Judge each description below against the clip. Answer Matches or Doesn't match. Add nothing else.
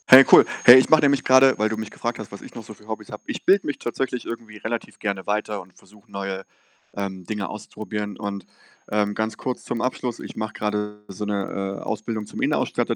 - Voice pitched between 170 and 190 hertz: Doesn't match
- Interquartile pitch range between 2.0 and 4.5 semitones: Matches